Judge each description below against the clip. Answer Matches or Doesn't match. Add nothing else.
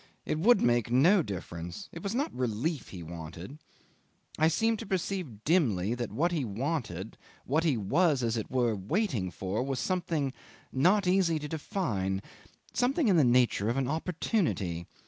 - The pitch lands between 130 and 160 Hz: Matches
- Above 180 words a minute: Doesn't match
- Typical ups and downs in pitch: Doesn't match